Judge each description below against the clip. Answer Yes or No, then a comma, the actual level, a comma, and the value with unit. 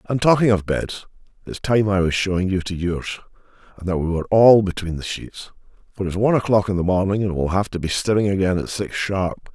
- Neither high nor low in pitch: No, very low, 95 Hz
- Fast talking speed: Yes, fast, 235 wpm